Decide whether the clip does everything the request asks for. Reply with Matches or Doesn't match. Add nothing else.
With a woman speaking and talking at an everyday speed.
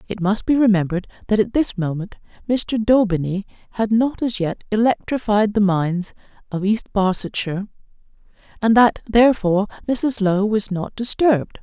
Matches